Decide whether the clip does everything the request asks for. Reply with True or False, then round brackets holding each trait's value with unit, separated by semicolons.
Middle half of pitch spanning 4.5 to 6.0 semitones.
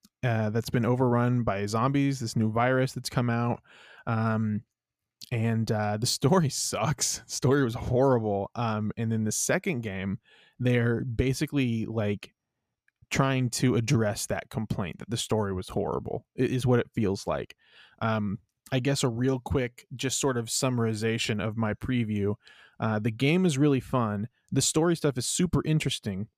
False (3.2 semitones)